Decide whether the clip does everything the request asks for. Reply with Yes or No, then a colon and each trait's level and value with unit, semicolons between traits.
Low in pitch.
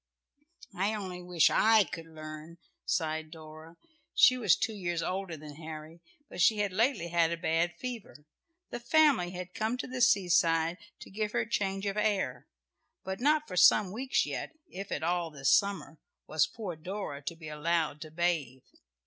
No: medium, 175 Hz